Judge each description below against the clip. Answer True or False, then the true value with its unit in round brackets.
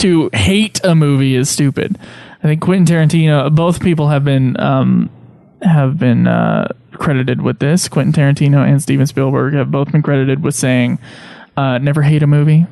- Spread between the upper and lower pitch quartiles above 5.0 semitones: False (2.9 semitones)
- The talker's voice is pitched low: False (145 Hz)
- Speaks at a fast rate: False (175 wpm)